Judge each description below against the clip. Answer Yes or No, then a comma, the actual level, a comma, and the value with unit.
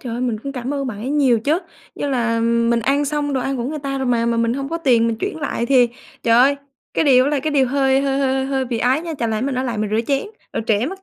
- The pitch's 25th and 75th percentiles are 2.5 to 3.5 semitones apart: Yes, average, 3.0 semitones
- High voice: Yes, very high, 265 Hz